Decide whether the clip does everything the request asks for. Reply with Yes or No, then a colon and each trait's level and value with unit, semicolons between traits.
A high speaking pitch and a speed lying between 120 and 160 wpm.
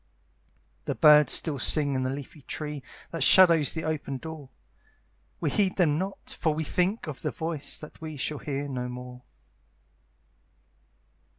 No: medium, 150 Hz; average, 155 wpm